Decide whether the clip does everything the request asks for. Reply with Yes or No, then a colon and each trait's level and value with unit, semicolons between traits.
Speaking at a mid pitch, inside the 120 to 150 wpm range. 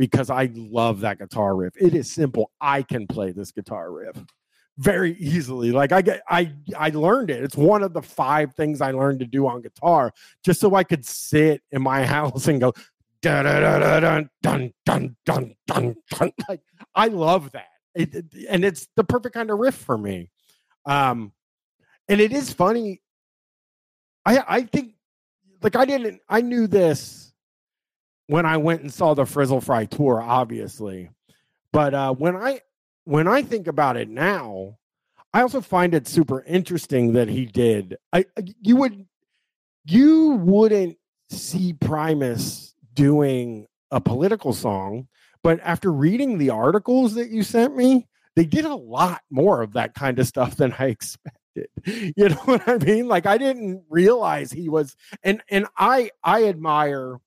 No: medium, 155 Hz; average, 165 wpm